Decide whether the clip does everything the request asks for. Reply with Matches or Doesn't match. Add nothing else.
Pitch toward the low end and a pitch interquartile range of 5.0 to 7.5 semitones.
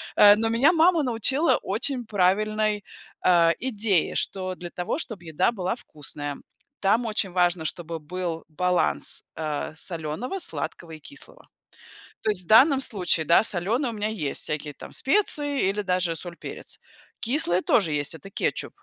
Doesn't match